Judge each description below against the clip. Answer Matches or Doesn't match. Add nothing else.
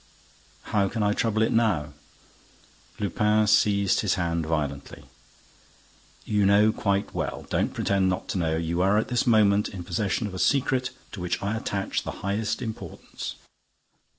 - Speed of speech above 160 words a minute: Doesn't match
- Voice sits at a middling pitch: Doesn't match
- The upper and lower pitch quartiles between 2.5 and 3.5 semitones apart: Matches